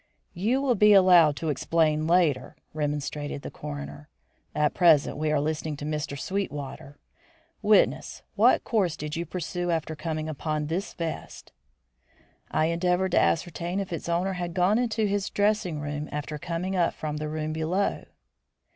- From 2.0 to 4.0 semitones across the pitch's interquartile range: Yes, average, 3.4 semitones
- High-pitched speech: No, medium, 160 Hz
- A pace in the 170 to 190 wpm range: No, average, 155 wpm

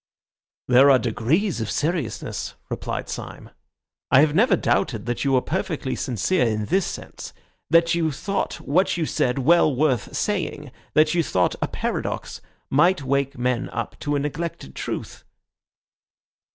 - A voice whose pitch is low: No, medium, 145 Hz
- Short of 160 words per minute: Yes, average, 150 wpm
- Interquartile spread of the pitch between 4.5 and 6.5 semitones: Yes, average, 5.2 semitones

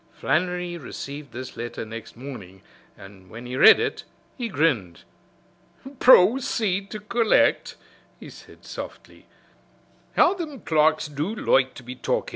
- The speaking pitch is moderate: Yes, medium, 150 Hz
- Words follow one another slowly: Yes, slow, 130 wpm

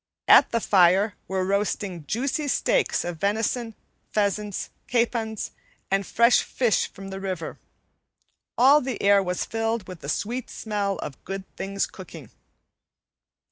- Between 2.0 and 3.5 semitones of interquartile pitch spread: Yes, average, 3.2 semitones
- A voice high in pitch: Yes, high, 205 Hz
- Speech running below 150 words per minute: Yes, slow, 135 wpm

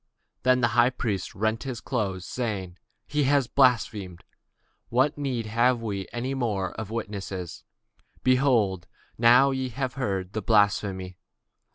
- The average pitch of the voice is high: No, low, 115 Hz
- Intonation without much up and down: No, average, 4.5 semitones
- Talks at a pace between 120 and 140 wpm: Yes, slow, 135 wpm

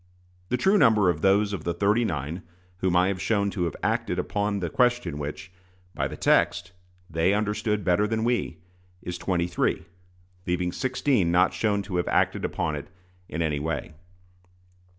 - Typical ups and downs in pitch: Yes, average, 3.7 semitones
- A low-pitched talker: Yes, very low, 95 Hz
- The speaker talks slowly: No, average, 170 wpm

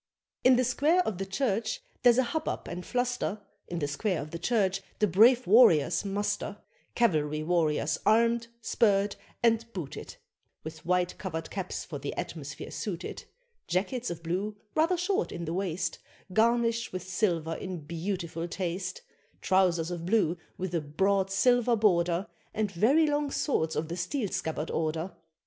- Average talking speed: Yes, average, 155 wpm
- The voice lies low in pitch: No, high, 190 Hz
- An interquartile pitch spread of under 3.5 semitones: No, wide, 5.5 semitones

